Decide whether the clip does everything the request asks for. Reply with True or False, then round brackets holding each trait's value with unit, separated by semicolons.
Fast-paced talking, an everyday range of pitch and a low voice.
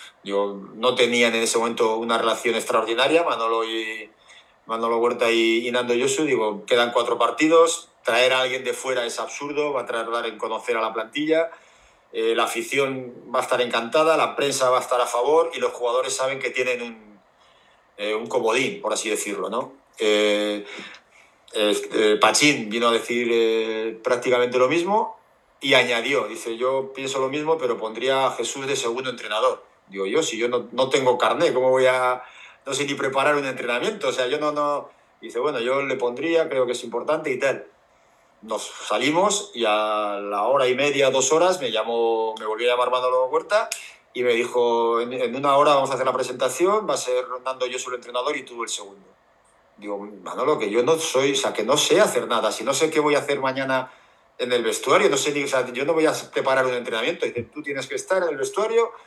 True (210 wpm; 3.4 semitones; 125 Hz)